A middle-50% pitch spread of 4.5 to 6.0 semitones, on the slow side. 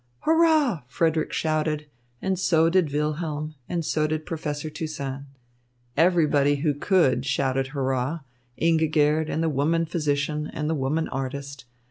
No: narrow, 2.4 semitones; slow, 130 wpm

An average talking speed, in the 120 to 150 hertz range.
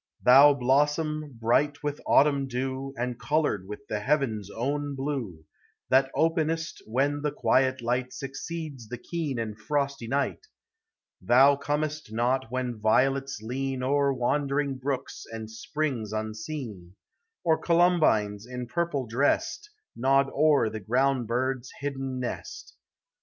No: slow, 125 wpm; low, 135 Hz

